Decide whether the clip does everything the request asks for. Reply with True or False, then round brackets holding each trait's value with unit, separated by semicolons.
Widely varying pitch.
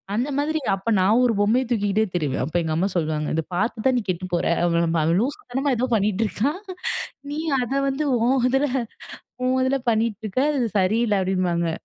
True (6.3 semitones)